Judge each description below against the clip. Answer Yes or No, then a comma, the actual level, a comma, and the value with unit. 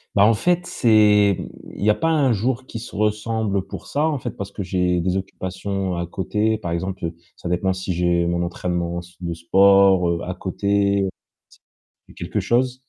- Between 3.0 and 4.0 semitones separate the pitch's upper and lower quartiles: Yes, average, 3.5 semitones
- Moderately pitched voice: No, low, 100 Hz